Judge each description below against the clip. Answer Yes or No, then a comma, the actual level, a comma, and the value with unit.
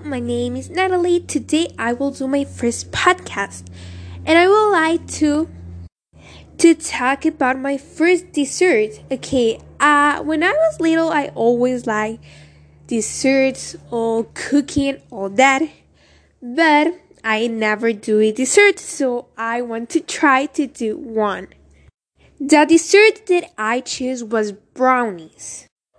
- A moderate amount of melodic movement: No, wide, 6.0 semitones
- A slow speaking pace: Yes, slow, 130 wpm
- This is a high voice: Yes, very high, 265 Hz